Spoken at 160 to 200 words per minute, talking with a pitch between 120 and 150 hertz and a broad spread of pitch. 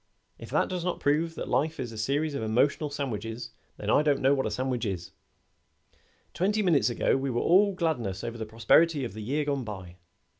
Yes: average, 195 wpm; low, 135 Hz; wide, 5.7 semitones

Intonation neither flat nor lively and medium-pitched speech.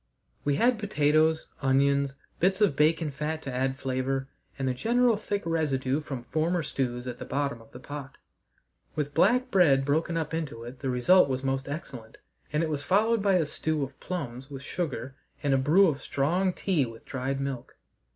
Yes: average, 3.8 semitones; medium, 145 Hz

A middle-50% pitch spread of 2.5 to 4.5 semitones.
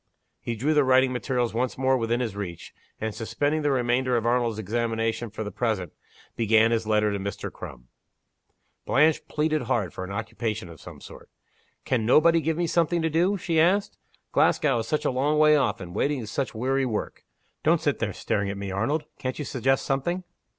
No: average, 5.0 semitones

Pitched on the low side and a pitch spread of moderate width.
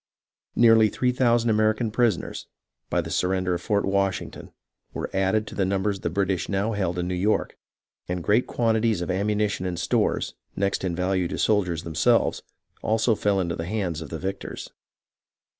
Yes: low, 100 Hz; average, 3.1 semitones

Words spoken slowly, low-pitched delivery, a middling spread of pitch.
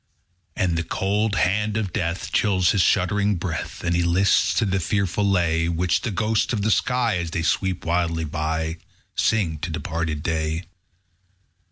No: average, 175 wpm; very low, 90 Hz; average, 3.6 semitones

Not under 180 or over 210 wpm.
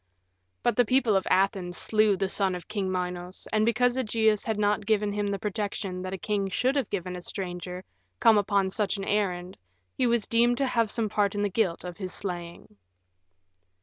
Yes: average, 200 wpm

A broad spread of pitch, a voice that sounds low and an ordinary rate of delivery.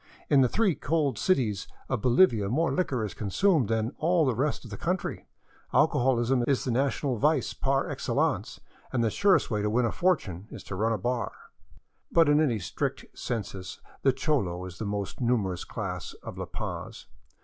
Yes: wide, 5.9 semitones; low, 120 Hz; average, 185 wpm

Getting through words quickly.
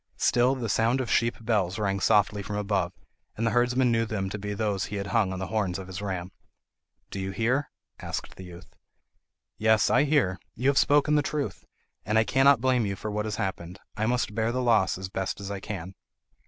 Yes: fast, 220 wpm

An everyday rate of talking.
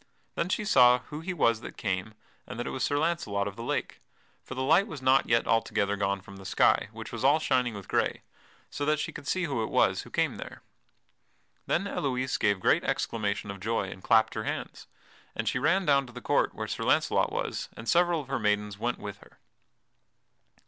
No: fast, 220 wpm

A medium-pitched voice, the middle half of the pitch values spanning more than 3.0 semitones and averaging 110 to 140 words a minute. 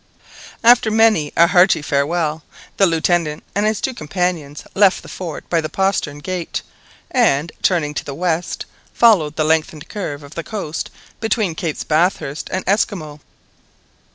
No: medium, 170 Hz; average, 4.1 semitones; average, 150 wpm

